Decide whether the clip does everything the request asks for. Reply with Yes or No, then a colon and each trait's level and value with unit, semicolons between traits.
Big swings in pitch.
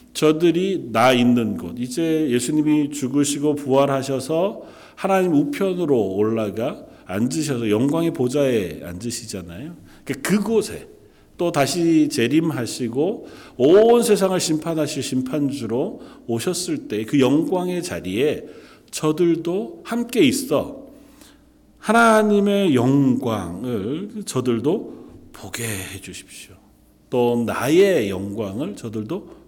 Yes: wide, 7.9 semitones